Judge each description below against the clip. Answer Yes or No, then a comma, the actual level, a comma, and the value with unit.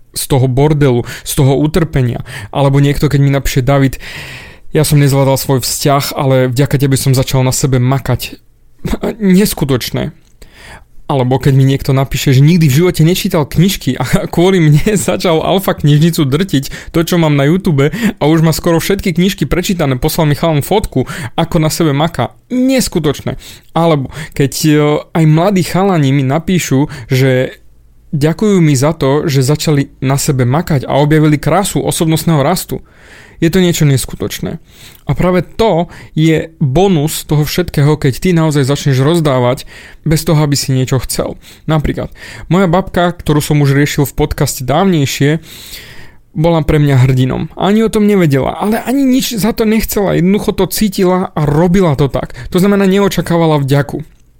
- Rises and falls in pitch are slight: No, average, 4.2 semitones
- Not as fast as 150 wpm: No, average, 160 wpm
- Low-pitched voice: No, medium, 155 Hz